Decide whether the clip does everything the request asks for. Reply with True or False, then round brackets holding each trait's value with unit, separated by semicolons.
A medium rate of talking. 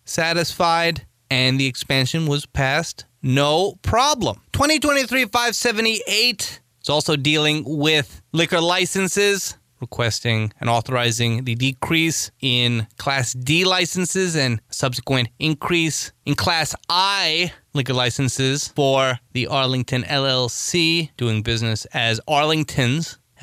False (105 wpm)